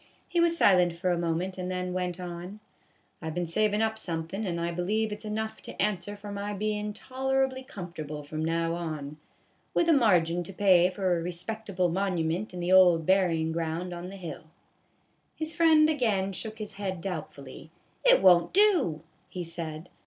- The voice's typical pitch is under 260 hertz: Yes, medium, 185 Hz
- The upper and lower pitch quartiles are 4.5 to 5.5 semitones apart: No, average, 4.0 semitones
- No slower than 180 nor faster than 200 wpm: Yes, average, 190 wpm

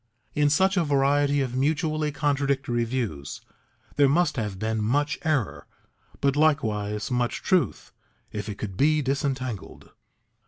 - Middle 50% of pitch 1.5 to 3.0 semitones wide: No, average, 4.8 semitones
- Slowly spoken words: Yes, slow, 130 wpm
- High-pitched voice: No, low, 135 Hz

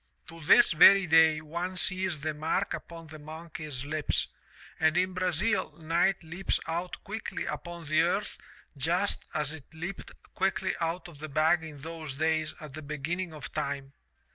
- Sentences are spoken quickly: No, average, 165 wpm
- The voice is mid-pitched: Yes, medium, 160 Hz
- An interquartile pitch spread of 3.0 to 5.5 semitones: No, narrow, 2.4 semitones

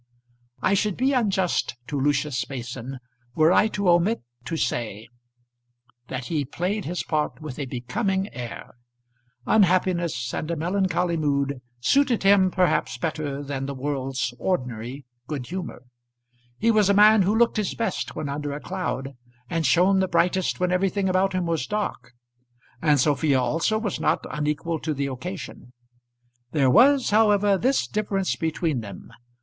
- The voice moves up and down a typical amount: No, wide, 5.8 semitones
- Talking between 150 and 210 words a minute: Yes, average, 155 wpm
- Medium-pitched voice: Yes, medium, 165 Hz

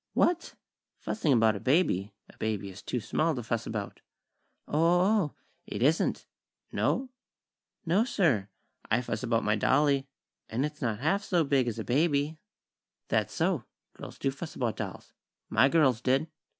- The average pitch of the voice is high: No, low, 135 Hz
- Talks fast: No, average, 165 wpm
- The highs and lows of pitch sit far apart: Yes, wide, 6.0 semitones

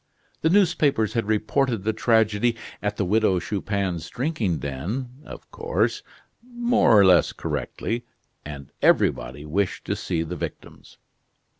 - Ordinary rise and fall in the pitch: No, wide, 5.9 semitones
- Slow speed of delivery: Yes, slow, 130 wpm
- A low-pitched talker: Yes, low, 110 Hz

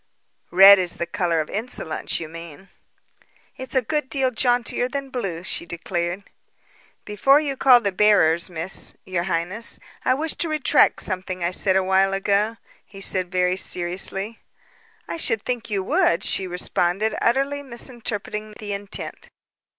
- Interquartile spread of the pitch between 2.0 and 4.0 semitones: No, average, 5.0 semitones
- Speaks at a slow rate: No, average, 150 wpm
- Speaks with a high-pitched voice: Yes, high, 195 Hz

